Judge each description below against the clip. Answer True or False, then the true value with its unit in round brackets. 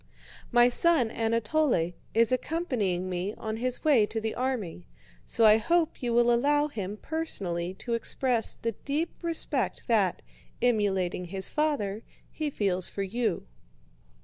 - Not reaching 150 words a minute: True (140 wpm)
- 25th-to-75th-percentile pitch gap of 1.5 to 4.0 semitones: False (5.4 semitones)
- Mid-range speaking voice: False (230 Hz)